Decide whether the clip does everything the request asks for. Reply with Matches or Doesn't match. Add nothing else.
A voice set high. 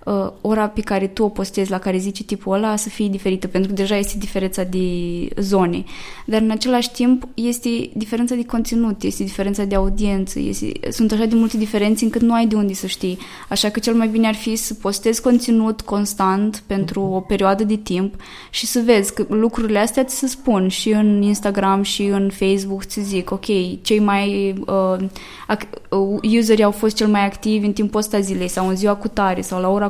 Matches